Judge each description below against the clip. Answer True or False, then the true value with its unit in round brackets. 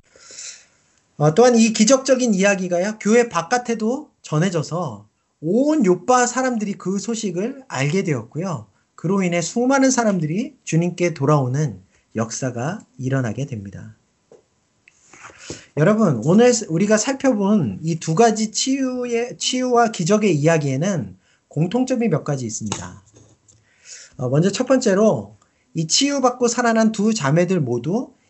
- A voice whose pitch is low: False (190 Hz)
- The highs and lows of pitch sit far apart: True (8.3 semitones)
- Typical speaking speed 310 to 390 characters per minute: False (275 characters per minute)